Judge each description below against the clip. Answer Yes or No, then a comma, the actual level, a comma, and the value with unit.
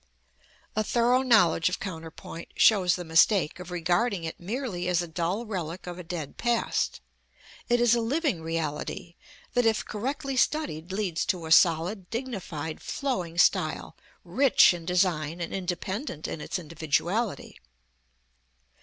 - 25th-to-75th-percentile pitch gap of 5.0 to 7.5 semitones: Yes, wide, 5.6 semitones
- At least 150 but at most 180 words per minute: No, average, 140 wpm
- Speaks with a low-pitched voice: No, medium, 180 Hz